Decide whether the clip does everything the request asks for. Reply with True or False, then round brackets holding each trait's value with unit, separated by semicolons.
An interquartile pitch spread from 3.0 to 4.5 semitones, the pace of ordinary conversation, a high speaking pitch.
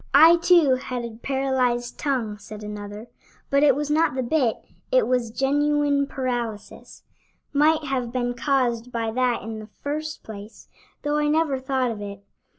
True (4.0 semitones; 160 wpm; 255 Hz)